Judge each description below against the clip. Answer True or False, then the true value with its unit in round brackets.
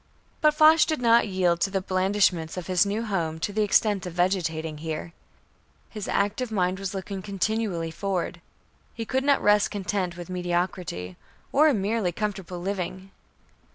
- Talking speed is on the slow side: False (160 wpm)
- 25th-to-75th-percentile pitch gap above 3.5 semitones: False (3.1 semitones)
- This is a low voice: False (190 Hz)